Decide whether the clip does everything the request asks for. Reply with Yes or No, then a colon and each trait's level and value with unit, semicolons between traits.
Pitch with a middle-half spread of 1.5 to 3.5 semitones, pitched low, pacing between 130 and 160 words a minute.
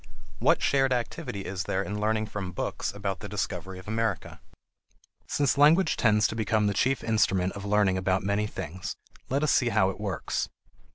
No: average, 2.8 semitones; low, 105 Hz; average, 180 wpm